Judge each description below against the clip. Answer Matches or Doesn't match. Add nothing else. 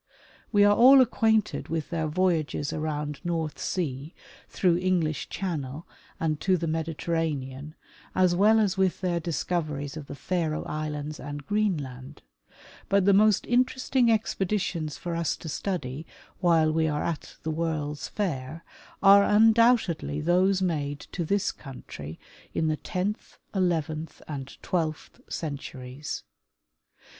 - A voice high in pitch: Doesn't match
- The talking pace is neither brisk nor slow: Doesn't match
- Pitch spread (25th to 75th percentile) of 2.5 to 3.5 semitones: Doesn't match